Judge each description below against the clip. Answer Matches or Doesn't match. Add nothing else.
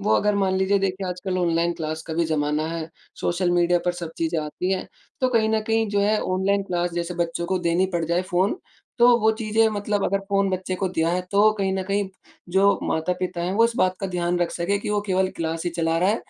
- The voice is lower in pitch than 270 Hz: Matches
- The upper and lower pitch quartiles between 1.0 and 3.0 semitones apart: Matches